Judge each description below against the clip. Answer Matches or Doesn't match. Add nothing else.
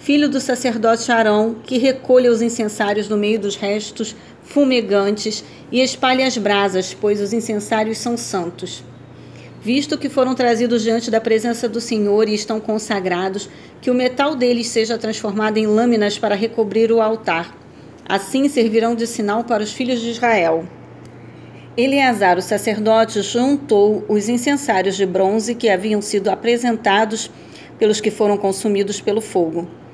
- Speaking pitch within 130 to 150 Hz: Doesn't match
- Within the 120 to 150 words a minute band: Matches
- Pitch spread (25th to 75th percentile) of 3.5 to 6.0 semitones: Doesn't match